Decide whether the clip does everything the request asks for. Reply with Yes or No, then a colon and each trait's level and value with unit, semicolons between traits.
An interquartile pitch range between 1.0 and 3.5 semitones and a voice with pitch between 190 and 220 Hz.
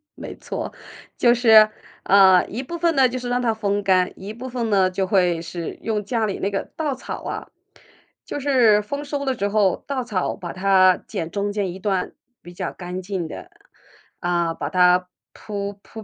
No: average, 4.4 semitones; high, 200 Hz